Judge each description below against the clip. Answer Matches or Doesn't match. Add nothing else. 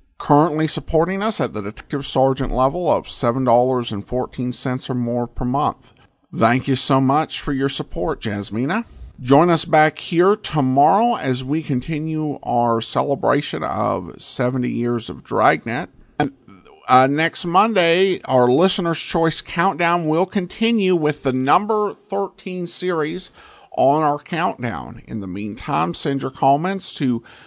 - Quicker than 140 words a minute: Doesn't match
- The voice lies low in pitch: Doesn't match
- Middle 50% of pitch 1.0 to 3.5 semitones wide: Doesn't match